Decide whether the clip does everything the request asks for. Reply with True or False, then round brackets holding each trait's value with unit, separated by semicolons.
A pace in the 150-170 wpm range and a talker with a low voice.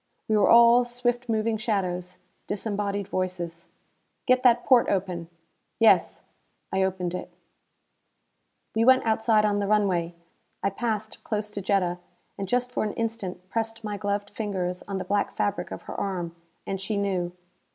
False (155 wpm; 205 Hz)